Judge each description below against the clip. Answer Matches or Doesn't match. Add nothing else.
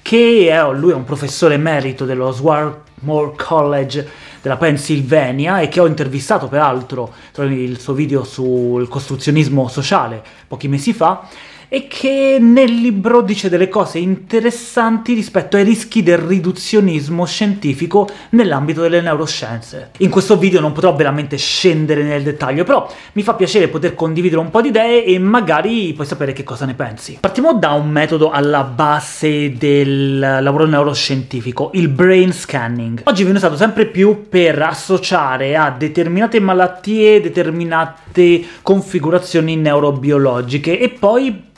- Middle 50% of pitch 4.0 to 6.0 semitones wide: Matches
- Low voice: Doesn't match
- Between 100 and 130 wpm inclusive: Doesn't match